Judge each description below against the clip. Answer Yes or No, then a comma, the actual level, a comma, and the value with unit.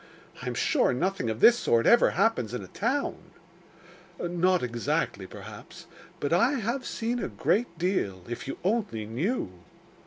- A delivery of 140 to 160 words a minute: Yes, average, 155 wpm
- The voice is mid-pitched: Yes, medium, 180 Hz